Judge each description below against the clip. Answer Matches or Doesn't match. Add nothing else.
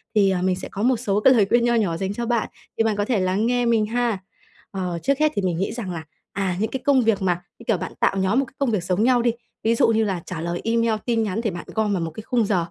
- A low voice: Doesn't match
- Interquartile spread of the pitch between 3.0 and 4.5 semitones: Matches